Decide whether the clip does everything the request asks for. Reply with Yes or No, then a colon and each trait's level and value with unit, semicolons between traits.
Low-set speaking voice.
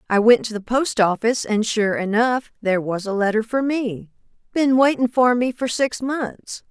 No: high, 230 Hz